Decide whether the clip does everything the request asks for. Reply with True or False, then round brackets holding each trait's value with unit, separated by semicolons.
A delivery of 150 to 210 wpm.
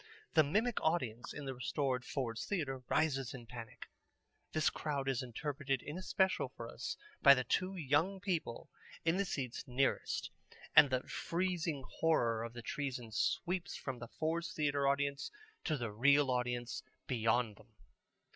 True (155 wpm)